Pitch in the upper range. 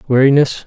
No: low, 135 Hz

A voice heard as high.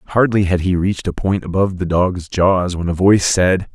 No: very low, 90 Hz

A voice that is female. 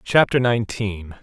No: male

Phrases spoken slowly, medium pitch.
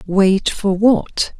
No: slow, 130 wpm; high, 200 Hz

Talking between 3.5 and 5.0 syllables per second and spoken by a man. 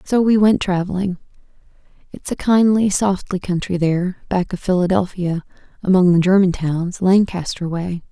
No: 4.9 syllables/s; female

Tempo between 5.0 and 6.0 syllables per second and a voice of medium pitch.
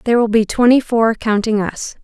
No: 5.4 syllables/s; high, 225 Hz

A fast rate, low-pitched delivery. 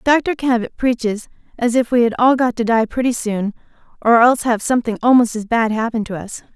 No: fast, 210 wpm; high, 235 Hz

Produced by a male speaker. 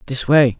Yes: male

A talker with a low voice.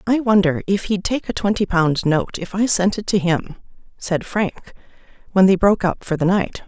No: high, 190 Hz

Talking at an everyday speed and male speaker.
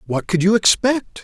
Yes: average, 195 wpm; male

